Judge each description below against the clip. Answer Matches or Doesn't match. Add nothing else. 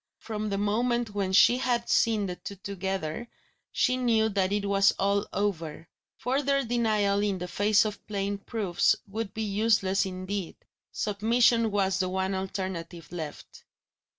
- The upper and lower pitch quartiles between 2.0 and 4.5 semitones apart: Matches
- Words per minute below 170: Matches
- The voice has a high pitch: Matches